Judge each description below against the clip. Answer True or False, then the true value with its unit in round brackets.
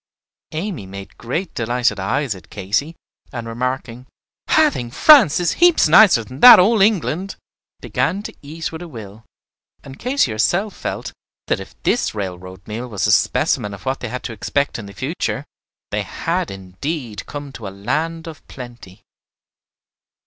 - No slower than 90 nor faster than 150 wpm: False (165 wpm)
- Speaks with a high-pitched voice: False (125 Hz)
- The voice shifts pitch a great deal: True (7.7 semitones)